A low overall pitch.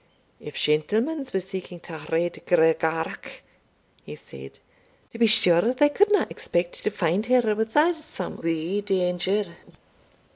No: high, 190 Hz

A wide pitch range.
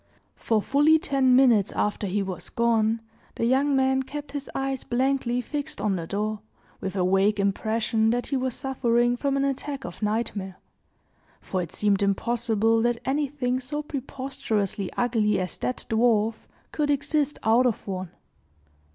No: average, 4.4 semitones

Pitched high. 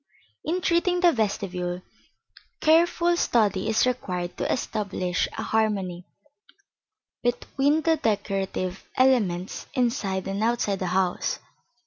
Yes: high, 215 Hz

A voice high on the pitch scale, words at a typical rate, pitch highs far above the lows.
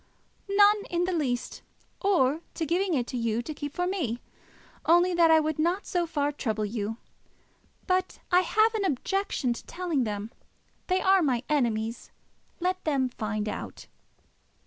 Yes: very high, 315 Hz; average, 155 wpm; wide, 7.1 semitones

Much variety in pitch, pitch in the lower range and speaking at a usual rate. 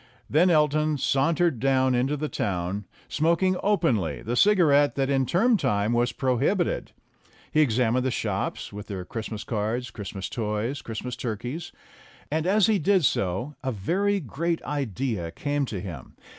Yes: wide, 6.1 semitones; low, 130 Hz; average, 150 wpm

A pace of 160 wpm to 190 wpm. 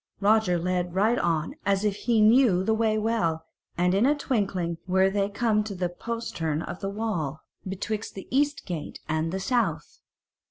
Yes: average, 175 wpm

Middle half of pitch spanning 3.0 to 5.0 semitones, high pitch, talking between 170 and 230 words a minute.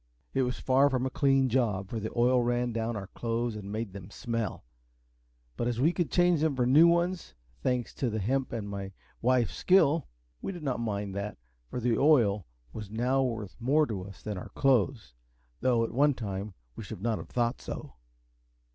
No: average, 4.0 semitones; low, 120 Hz; average, 200 wpm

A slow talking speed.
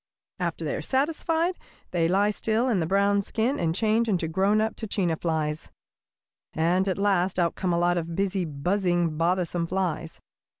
No: average, 170 wpm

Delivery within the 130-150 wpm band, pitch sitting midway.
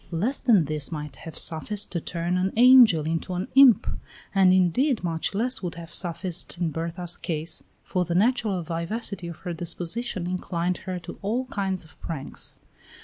No: average, 170 wpm; medium, 180 Hz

